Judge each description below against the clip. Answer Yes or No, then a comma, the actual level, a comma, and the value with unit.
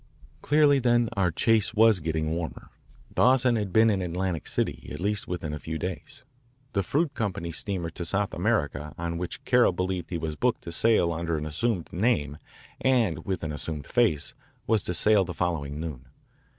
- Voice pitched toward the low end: Yes, very low, 90 Hz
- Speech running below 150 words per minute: No, average, 180 wpm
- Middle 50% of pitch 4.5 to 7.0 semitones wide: Yes, wide, 5.6 semitones